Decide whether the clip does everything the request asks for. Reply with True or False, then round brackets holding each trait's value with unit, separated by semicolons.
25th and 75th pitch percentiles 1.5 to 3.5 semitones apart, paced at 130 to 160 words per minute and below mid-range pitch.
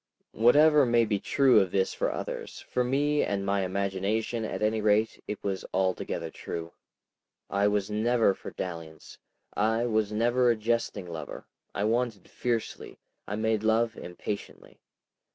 True (3.0 semitones; 150 wpm; 110 Hz)